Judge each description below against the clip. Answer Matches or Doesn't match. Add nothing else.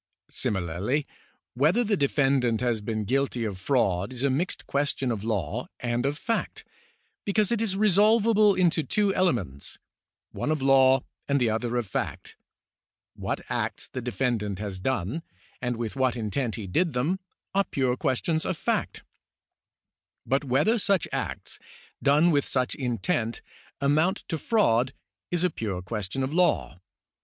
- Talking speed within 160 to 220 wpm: Doesn't match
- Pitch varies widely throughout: Matches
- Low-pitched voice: Matches